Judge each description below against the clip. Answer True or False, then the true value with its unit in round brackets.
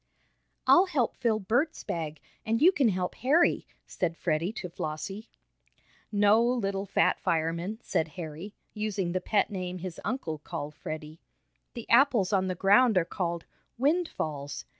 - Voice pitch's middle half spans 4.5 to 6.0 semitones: True (5.5 semitones)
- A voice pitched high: True (195 Hz)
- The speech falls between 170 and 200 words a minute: False (145 wpm)